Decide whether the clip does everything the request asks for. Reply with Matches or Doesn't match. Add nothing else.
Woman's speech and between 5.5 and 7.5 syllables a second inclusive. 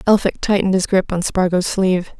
Matches